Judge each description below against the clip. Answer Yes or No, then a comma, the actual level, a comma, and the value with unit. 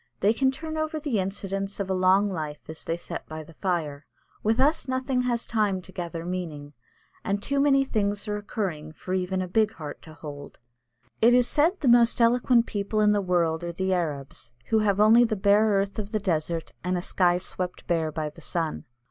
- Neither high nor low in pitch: No, high, 195 Hz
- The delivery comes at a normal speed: No, fast, 210 wpm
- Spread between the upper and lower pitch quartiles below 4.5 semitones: No, average, 4.8 semitones